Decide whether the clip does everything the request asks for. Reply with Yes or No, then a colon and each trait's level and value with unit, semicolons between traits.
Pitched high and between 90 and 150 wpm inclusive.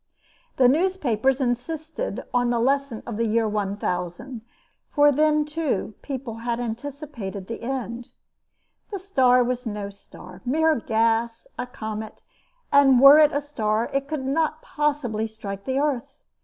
Yes: very high, 250 Hz; average, 140 wpm